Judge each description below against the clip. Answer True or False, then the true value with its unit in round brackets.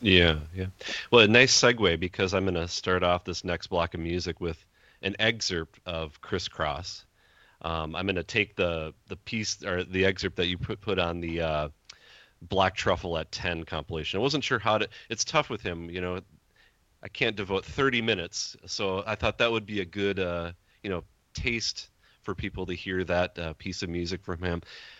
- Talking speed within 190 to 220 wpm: True (205 wpm)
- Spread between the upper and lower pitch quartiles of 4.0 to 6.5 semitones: False (2.8 semitones)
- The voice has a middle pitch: False (90 Hz)